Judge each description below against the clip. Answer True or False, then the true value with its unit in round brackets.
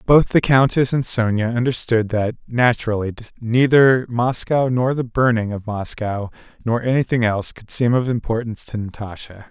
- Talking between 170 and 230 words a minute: False (150 wpm)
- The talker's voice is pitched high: False (120 Hz)